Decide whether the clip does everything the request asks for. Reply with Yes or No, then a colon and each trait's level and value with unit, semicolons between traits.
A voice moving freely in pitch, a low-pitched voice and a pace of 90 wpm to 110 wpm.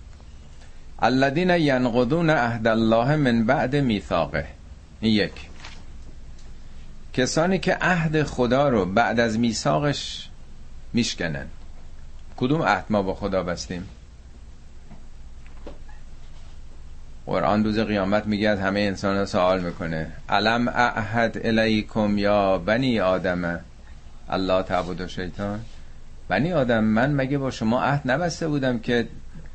Yes: wide, 7.8 semitones; very low, 95 Hz; slow, 105 wpm